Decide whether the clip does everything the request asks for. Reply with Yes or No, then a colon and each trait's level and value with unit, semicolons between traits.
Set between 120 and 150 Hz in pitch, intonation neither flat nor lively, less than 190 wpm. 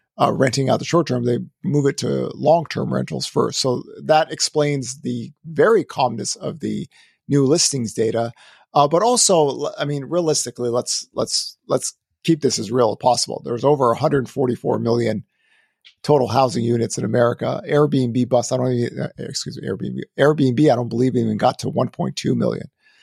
Yes: low, 135 Hz; average, 3.7 semitones; average, 175 wpm